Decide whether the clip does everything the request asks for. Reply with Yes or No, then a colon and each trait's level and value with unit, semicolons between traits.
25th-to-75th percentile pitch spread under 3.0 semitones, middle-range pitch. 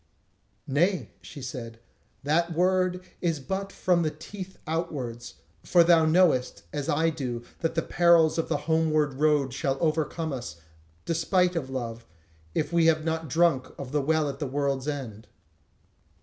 No: average, 3.9 semitones; medium, 155 Hz